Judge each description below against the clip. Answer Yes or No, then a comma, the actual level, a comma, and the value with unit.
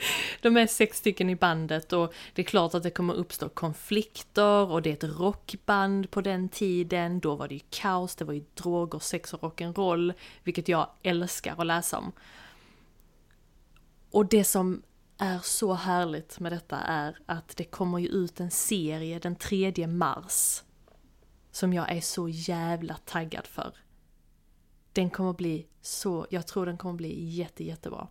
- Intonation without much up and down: Yes, narrow, 2.3 semitones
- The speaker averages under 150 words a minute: No, average, 165 wpm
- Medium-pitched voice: Yes, medium, 175 Hz